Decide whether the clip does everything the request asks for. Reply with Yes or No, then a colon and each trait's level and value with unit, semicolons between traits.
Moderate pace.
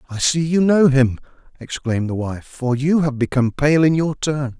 No: fast, 210 wpm